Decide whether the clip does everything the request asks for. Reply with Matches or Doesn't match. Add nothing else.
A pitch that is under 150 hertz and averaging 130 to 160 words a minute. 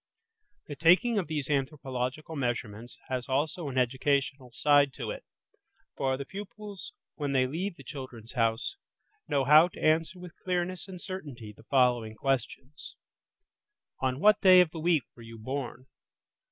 Matches